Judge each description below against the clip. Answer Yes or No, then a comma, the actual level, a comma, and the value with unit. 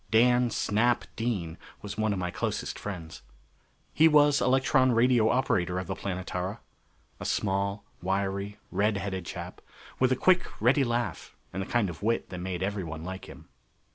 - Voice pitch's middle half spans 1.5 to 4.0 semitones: No, average, 4.6 semitones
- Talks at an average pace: Yes, average, 165 wpm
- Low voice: Yes, low, 105 Hz